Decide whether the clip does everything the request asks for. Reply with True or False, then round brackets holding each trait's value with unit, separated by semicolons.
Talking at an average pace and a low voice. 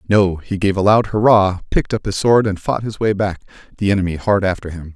False (240 wpm; 100 Hz)